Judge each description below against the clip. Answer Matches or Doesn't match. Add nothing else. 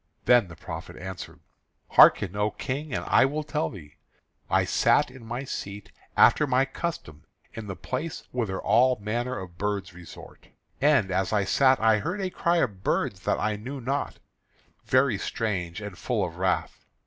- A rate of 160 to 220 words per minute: Matches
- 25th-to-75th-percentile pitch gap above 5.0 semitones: Matches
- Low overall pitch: Matches